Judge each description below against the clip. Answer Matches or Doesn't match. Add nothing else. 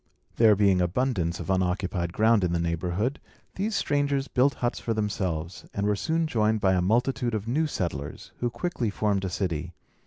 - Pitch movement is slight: Doesn't match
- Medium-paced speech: Matches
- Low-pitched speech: Matches